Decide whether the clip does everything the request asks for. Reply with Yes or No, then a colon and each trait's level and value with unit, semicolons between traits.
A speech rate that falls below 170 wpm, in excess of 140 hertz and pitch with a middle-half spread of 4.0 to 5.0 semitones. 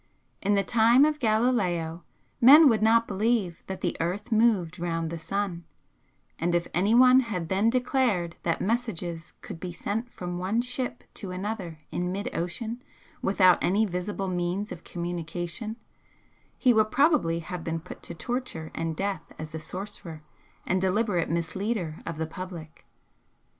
Yes: average, 155 wpm; high, 190 Hz; average, 4.7 semitones